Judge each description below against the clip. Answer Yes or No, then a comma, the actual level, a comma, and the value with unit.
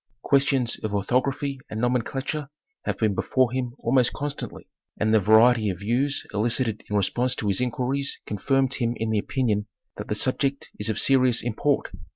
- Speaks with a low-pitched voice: Yes, low, 125 Hz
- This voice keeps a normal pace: Yes, average, 170 wpm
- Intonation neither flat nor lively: Yes, average, 3.7 semitones